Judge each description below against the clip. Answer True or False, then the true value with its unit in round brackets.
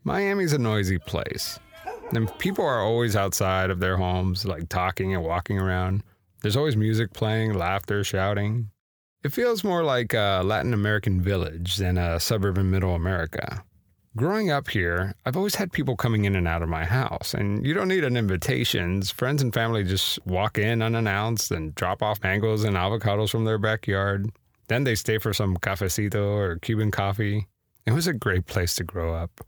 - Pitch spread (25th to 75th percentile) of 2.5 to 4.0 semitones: True (3.3 semitones)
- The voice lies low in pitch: True (105 Hz)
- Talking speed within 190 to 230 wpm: False (180 wpm)